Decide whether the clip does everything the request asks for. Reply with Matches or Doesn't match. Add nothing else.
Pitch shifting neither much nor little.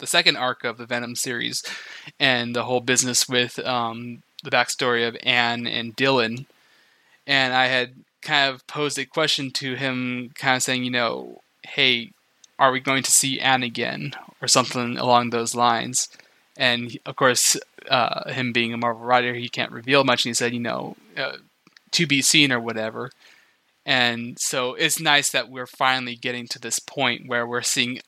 Doesn't match